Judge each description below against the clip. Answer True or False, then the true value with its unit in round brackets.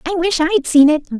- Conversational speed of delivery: False (300 wpm)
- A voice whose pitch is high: True (325 Hz)